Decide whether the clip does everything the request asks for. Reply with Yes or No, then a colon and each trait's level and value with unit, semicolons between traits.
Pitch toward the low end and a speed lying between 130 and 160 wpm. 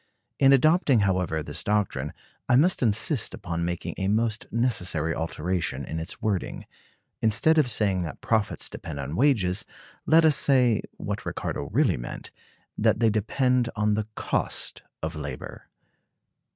Yes: low, 105 Hz; average, 145 wpm